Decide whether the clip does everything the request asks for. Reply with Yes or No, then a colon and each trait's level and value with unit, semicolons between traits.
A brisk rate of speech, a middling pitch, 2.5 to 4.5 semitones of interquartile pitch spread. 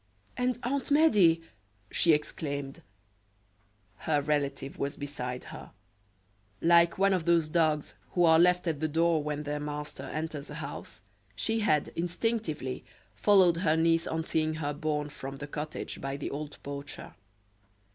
No: average, 145 wpm; medium, 155 Hz; average, 2.8 semitones